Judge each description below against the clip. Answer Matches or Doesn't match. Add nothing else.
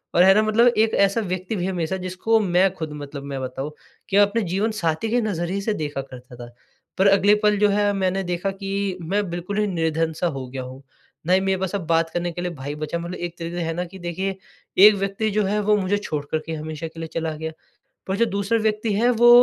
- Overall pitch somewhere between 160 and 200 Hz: Matches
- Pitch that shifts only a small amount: Doesn't match